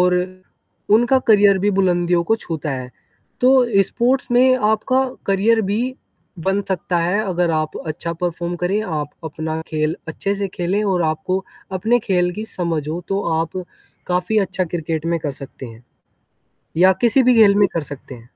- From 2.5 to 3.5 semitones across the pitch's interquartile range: No, average, 4.1 semitones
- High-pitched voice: No, medium, 180 Hz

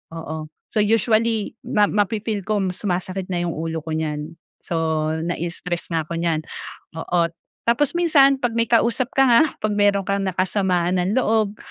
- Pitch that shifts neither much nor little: Yes, average, 4.8 semitones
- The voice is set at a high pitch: Yes, high, 195 Hz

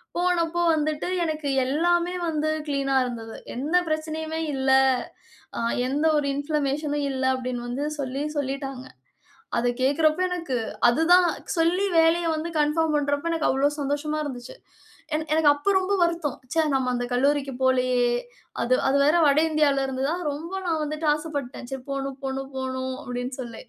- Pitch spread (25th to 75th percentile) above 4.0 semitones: No, average, 3.1 semitones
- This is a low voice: No, very high, 290 Hz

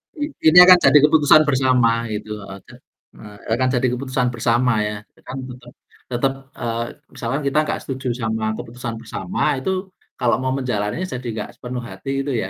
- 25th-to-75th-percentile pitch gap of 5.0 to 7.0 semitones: No, average, 2.9 semitones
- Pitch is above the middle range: No, low, 125 Hz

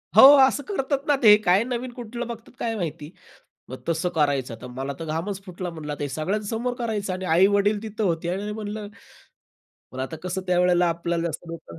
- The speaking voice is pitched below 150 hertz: No, medium, 185 Hz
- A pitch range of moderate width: Yes, average, 4.8 semitones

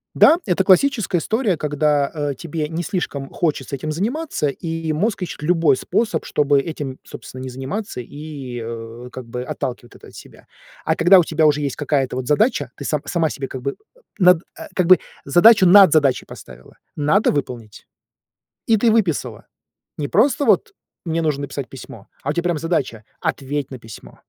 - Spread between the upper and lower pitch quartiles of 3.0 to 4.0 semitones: No, average, 4.8 semitones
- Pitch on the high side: No, medium, 150 Hz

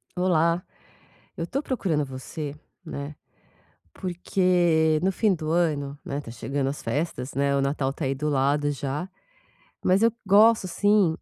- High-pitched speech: No, medium, 155 Hz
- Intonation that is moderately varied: Yes, average, 4.4 semitones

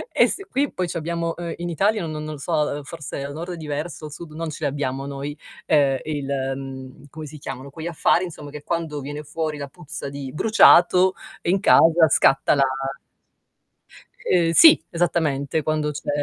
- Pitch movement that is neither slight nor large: Yes, average, 3.1 semitones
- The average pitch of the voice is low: No, medium, 155 Hz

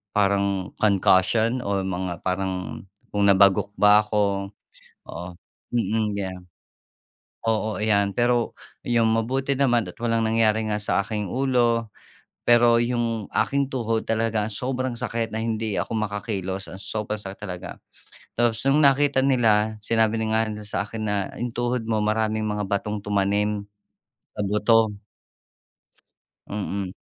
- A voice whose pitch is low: Yes, low, 110 Hz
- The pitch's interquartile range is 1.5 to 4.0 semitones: Yes, narrow, 2.5 semitones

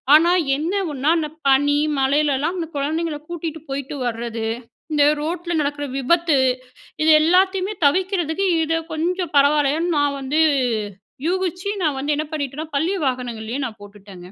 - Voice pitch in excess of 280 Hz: Yes, very high, 300 Hz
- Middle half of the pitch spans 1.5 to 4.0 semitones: Yes, average, 3.7 semitones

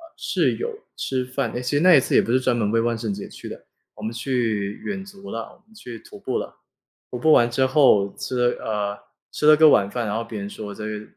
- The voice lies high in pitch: No, low, 120 Hz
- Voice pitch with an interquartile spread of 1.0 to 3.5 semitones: No, average, 4.0 semitones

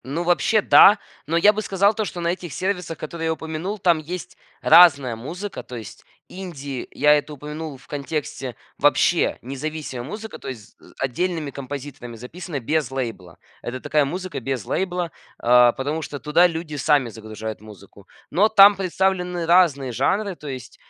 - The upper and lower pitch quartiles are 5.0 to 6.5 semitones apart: Yes, wide, 5.5 semitones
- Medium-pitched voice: Yes, medium, 155 Hz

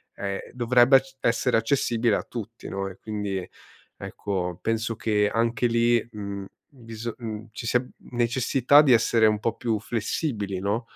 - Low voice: Yes, low, 115 Hz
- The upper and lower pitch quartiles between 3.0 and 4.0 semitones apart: No, narrow, 2.5 semitones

